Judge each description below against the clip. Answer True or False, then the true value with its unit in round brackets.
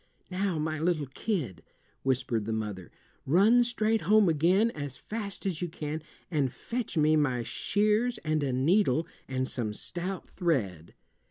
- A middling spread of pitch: False (7.4 semitones)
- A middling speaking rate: True (150 wpm)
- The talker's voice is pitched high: False (155 Hz)